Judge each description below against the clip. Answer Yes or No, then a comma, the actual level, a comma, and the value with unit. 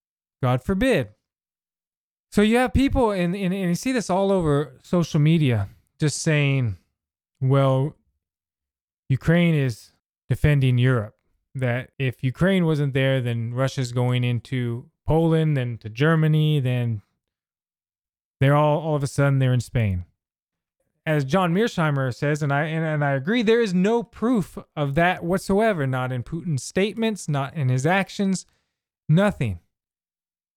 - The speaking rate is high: No, average, 145 wpm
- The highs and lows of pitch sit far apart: Yes, wide, 5.9 semitones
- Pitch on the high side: No, medium, 140 Hz